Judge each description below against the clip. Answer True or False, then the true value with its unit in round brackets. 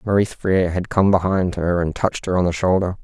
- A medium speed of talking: False (240 wpm)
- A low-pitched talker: True (90 Hz)